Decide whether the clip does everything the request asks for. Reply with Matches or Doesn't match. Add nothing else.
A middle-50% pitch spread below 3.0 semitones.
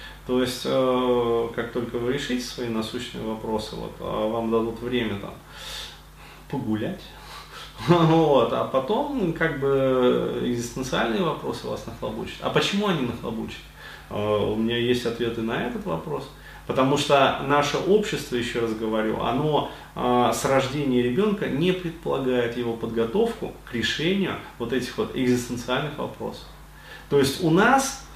Doesn't match